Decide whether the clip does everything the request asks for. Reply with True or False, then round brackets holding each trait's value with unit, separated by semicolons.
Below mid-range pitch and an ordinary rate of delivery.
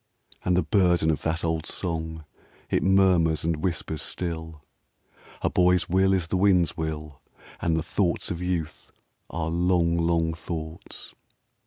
True (85 Hz; 145 wpm)